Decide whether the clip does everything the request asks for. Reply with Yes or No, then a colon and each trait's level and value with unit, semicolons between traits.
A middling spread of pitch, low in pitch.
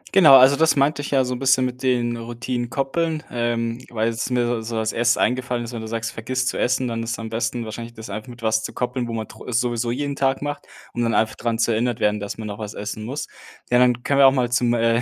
No: narrow, 2.0 semitones; low, 120 Hz